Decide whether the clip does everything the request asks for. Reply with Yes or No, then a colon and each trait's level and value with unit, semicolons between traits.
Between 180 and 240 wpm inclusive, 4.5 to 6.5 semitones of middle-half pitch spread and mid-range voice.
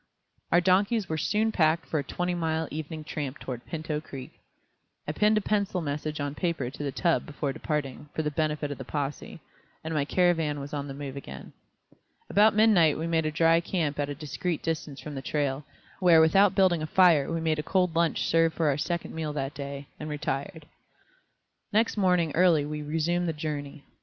No: average, 200 wpm; average, 2.9 semitones; medium, 155 Hz